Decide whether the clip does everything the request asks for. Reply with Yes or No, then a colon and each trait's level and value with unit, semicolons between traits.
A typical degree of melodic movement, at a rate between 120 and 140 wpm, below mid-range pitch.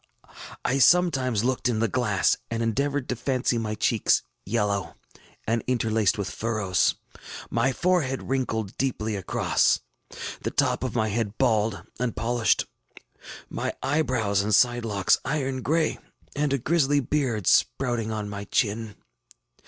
Yes: average, 3.6 semitones; slow, 135 wpm; low, 115 Hz